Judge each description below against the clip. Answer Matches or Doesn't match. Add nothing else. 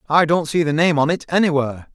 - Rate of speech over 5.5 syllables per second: Matches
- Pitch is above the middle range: Doesn't match